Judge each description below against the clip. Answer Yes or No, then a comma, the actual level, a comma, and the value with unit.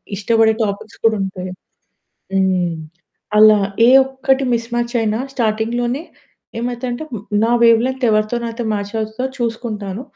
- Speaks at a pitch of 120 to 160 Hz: No, high, 225 Hz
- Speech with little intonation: Yes, narrow, 2.3 semitones